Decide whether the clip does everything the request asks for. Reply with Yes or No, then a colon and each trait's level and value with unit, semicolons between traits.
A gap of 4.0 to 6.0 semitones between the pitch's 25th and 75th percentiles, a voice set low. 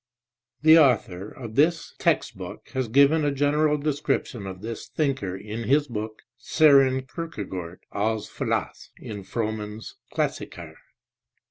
Yes: wide, 5.4 semitones; low, 125 Hz